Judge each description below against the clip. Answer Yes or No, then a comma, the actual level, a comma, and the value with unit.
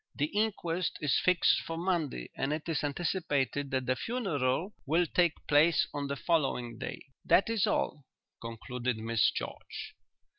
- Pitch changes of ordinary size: Yes, average, 5.0 semitones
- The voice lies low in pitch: No, medium, 150 Hz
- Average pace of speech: Yes, average, 150 wpm